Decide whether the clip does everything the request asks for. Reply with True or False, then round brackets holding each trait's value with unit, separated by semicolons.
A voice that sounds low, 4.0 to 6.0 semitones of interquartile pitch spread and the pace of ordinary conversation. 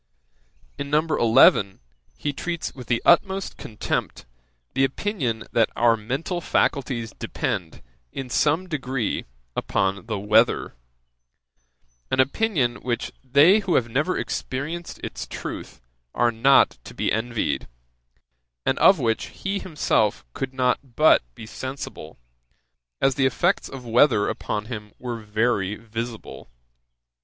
False (125 Hz; 4.4 semitones; 125 wpm)